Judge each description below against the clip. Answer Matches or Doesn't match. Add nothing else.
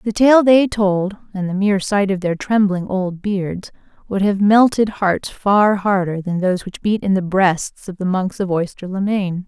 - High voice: Matches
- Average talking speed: Doesn't match